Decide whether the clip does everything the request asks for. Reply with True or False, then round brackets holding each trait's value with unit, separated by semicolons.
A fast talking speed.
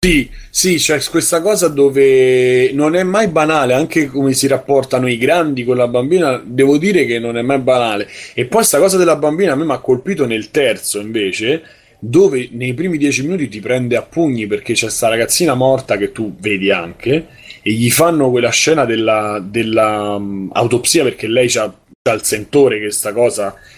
True (190 wpm)